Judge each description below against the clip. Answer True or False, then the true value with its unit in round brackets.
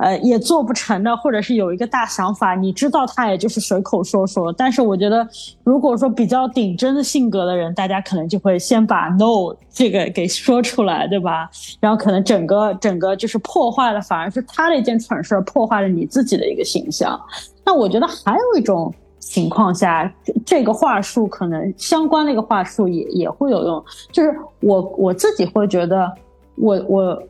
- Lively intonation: False (4.6 semitones)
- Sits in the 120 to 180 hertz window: False (210 Hz)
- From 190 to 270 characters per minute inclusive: False (295 characters per minute)